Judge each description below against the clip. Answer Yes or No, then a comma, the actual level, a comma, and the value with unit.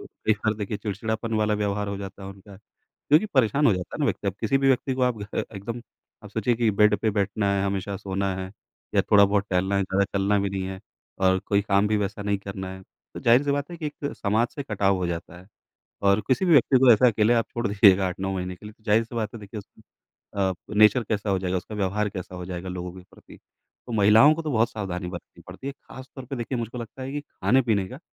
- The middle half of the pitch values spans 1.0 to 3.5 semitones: Yes, average, 3.2 semitones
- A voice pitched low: Yes, low, 105 Hz